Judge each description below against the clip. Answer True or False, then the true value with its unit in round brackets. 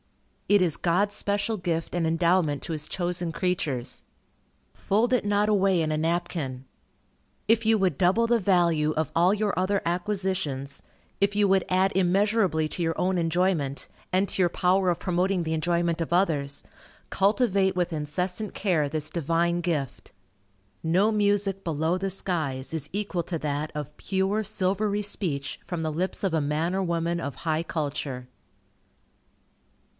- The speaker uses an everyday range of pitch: True (3.5 semitones)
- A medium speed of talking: True (160 wpm)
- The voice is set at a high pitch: False (175 Hz)